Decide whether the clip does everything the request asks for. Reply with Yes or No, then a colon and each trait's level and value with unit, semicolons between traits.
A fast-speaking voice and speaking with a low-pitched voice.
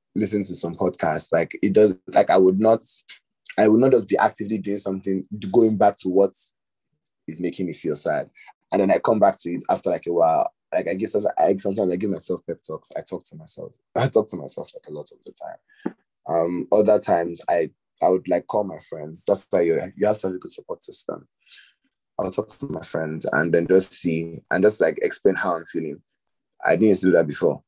Yes: fast, 235 wpm; low, 105 Hz